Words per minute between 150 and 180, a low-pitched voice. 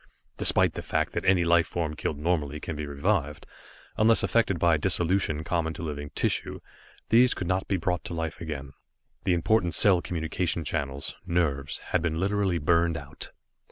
Yes: average, 170 wpm; very low, 85 Hz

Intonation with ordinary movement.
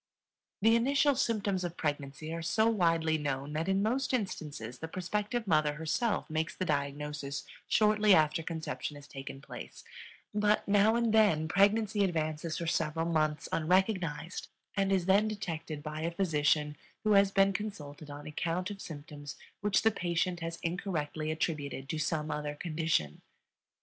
Yes: average, 4.8 semitones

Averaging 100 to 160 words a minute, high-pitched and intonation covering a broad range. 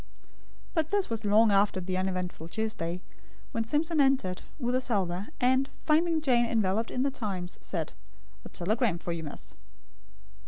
Yes: average, 155 wpm; high, 220 Hz; wide, 6.0 semitones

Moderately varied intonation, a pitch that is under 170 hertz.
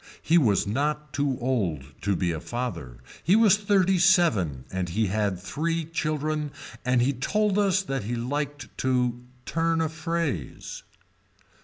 No: wide, 7.7 semitones; medium, 140 Hz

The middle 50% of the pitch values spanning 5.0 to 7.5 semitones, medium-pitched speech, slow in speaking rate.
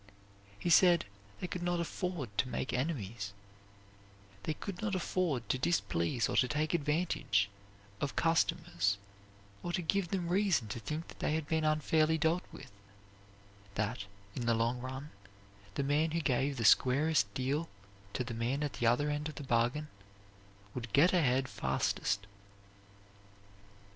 No: wide, 5.6 semitones; medium, 145 Hz; average, 155 wpm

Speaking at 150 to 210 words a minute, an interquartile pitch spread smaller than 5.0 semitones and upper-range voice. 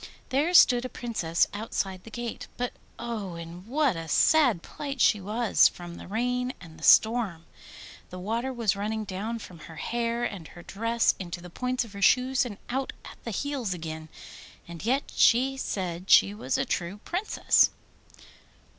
No: average, 170 wpm; wide, 5.4 semitones; high, 220 Hz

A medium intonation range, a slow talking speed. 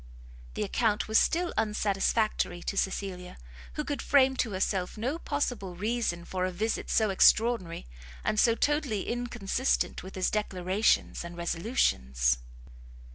Yes: average, 4.6 semitones; slow, 130 wpm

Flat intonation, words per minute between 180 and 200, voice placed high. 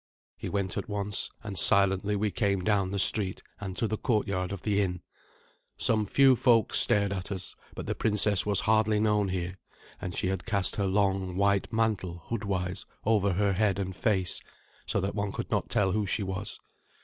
No: narrow, 1.9 semitones; average, 190 wpm; low, 100 Hz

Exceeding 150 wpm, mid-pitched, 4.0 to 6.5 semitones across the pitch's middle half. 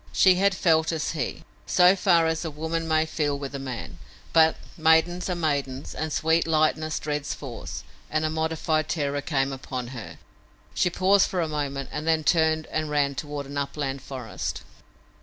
No: average, 175 wpm; medium, 155 Hz; narrow, 2.4 semitones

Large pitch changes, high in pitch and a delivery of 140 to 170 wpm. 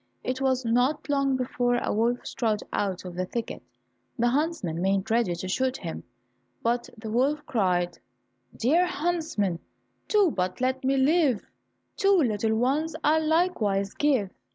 Yes: wide, 6.2 semitones; high, 245 Hz; average, 150 wpm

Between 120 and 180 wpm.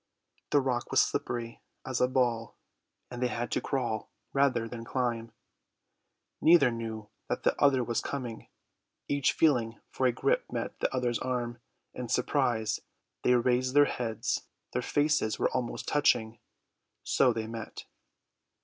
Yes: average, 145 wpm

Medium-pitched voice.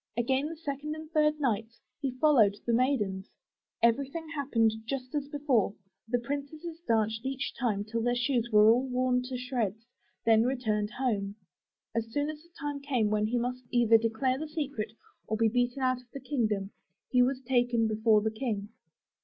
No: high, 245 Hz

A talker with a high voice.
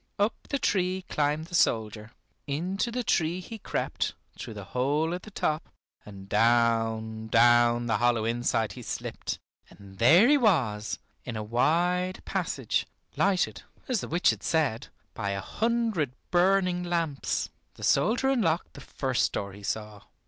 No: medium, 145 Hz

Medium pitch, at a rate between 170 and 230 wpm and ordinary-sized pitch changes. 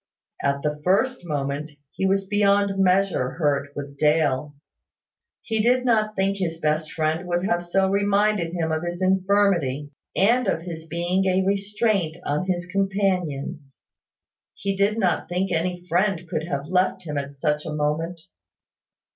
No: medium, 175 Hz; average, 155 wpm; average, 4.2 semitones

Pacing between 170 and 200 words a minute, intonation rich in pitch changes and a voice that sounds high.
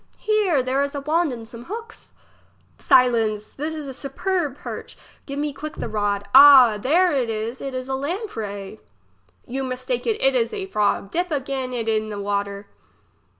Yes: average, 175 wpm; wide, 6.0 semitones; very high, 265 Hz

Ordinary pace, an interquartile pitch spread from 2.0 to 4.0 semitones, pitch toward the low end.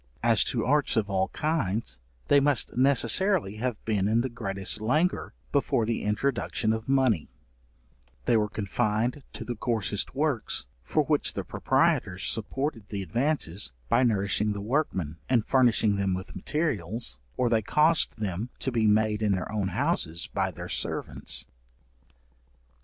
No: average, 150 wpm; average, 4.5 semitones; low, 110 Hz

